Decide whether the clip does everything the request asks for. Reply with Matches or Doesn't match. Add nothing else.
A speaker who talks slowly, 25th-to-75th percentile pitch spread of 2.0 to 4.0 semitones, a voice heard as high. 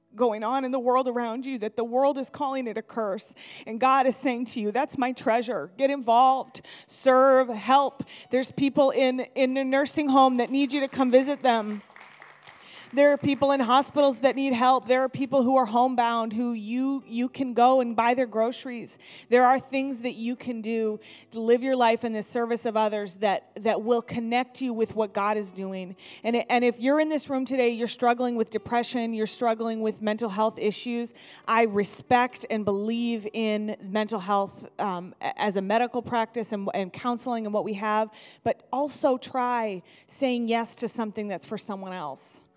Doesn't match